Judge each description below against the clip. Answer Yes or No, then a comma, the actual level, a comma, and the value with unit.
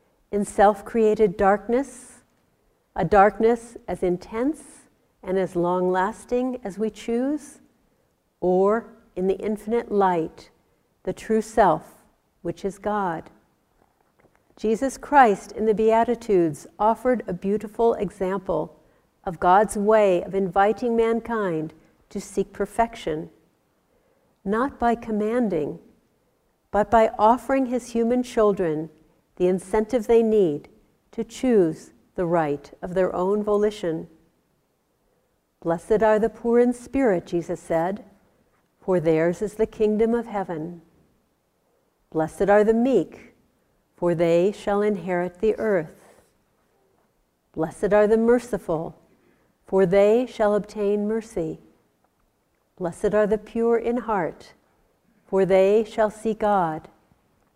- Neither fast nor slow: No, slow, 115 wpm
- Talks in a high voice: Yes, high, 210 Hz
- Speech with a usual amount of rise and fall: Yes, average, 3.7 semitones